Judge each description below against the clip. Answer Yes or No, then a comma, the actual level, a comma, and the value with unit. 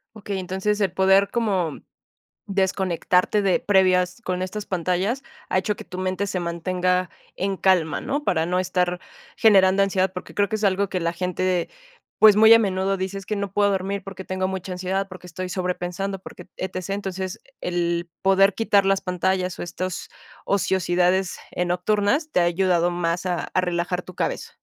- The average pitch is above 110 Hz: Yes, medium, 185 Hz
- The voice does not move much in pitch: Yes, narrow, 1.5 semitones